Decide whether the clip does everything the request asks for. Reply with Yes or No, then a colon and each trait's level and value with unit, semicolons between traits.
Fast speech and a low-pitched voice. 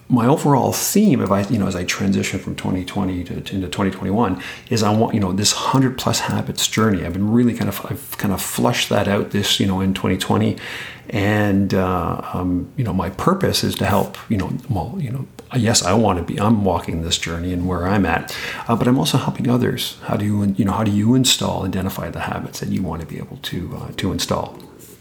Yes: fast, 230 wpm; low, 100 Hz